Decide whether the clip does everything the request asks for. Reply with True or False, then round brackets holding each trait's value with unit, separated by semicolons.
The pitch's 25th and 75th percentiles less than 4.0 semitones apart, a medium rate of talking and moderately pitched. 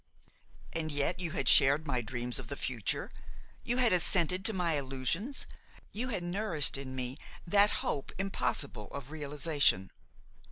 False (5.4 semitones; 150 wpm; 150 Hz)